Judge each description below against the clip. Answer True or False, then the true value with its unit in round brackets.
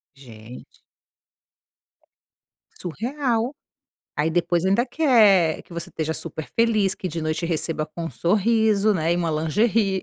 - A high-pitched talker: False (175 Hz)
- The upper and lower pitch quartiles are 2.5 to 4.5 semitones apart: False (5.4 semitones)